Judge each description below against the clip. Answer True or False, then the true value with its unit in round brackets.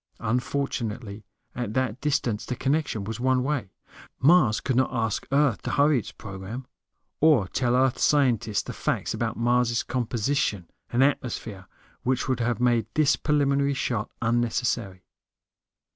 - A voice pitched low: True (125 Hz)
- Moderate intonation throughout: True (3.5 semitones)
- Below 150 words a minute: True (140 wpm)